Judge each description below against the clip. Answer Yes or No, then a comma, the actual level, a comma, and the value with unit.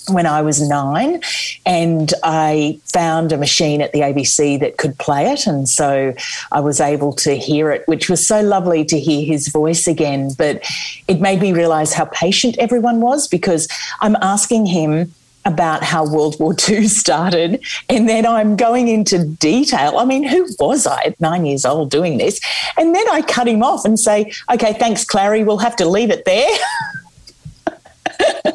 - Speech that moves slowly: No, average, 180 wpm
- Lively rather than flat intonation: Yes, wide, 6.4 semitones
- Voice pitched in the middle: Yes, medium, 175 Hz